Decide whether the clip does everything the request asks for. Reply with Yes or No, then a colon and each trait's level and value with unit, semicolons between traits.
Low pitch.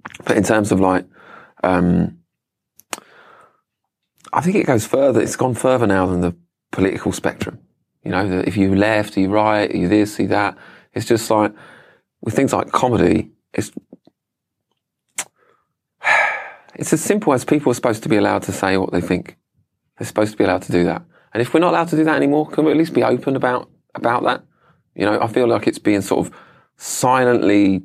Yes: low, 105 Hz